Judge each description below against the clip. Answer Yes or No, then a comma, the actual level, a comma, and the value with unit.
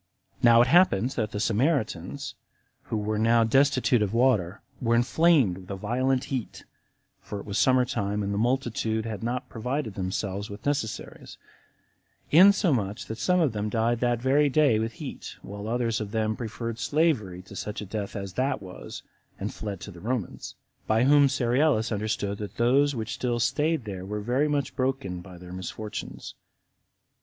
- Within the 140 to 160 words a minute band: No, average, 170 wpm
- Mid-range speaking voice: No, low, 115 Hz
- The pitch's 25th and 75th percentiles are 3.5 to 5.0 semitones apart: Yes, average, 4.2 semitones